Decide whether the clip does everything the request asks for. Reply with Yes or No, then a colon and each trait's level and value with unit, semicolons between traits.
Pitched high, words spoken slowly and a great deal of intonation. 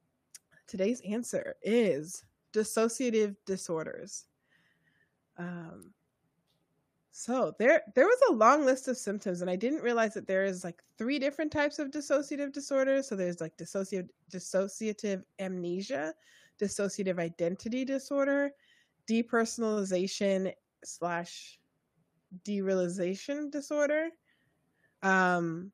Yes: high, 210 Hz; slow, 100 wpm; wide, 6.6 semitones